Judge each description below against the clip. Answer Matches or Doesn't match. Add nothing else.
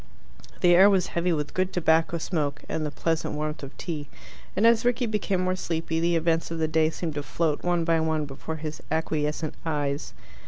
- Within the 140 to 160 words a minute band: Doesn't match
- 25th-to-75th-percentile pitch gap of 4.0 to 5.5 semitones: Doesn't match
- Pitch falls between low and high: Matches